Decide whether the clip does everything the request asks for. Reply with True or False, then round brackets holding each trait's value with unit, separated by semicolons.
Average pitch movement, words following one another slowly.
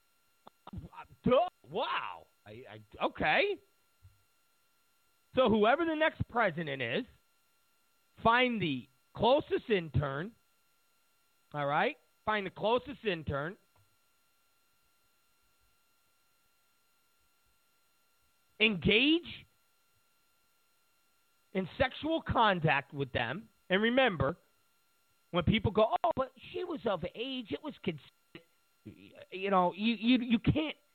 False (7.6 semitones; 95 wpm)